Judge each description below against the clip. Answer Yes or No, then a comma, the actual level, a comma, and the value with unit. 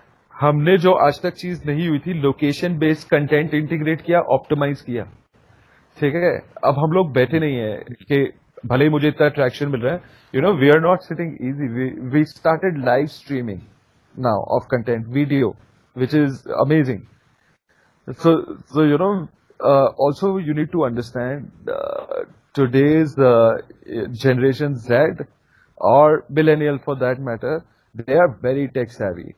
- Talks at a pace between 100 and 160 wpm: Yes, average, 145 wpm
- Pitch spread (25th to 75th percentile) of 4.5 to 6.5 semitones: No, average, 3.6 semitones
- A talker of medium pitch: Yes, medium, 145 Hz